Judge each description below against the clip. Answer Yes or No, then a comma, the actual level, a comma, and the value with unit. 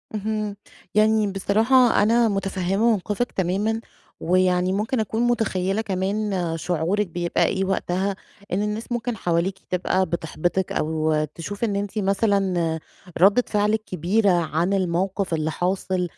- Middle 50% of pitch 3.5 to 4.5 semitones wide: No, average, 2.9 semitones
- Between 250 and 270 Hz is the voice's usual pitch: No, high, 195 Hz